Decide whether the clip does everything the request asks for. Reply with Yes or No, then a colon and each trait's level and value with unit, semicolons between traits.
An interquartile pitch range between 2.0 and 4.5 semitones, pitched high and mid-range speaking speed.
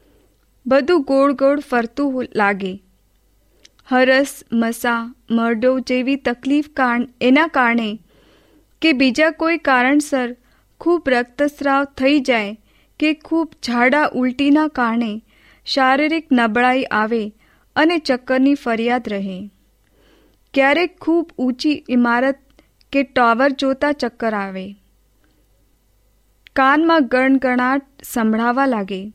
No: average, 3.5 semitones; very high, 255 Hz; slow, 95 wpm